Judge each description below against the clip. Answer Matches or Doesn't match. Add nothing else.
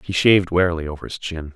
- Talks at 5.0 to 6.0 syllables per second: Doesn't match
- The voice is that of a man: Matches